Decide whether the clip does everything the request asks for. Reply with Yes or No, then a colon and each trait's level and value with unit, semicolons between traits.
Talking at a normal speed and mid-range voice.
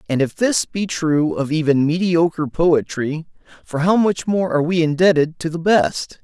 Yes: average, 185 wpm; medium, 165 Hz